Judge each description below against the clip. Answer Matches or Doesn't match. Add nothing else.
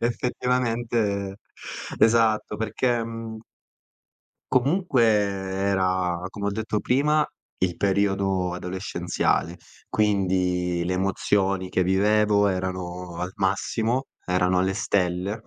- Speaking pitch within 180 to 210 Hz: Doesn't match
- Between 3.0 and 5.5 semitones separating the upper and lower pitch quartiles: Matches